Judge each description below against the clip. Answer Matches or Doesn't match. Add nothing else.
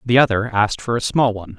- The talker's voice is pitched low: Matches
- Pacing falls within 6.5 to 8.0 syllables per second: Matches